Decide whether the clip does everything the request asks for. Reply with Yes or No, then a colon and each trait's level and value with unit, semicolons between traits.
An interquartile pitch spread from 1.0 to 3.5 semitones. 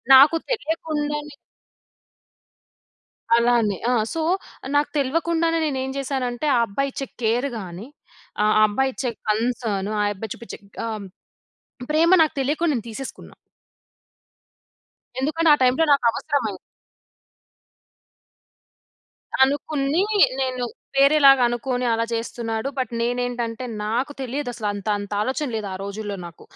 No: average, 4.2 semitones